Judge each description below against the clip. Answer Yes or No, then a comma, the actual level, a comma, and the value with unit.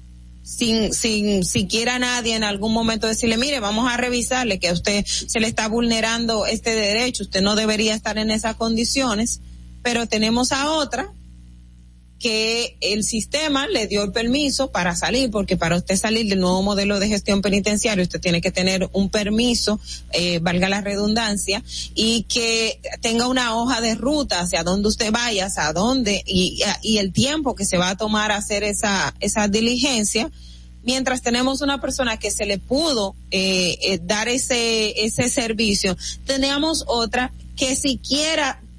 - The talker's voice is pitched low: No, high, 220 Hz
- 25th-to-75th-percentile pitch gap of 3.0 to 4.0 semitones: Yes, average, 3.6 semitones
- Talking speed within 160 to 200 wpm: Yes, average, 165 wpm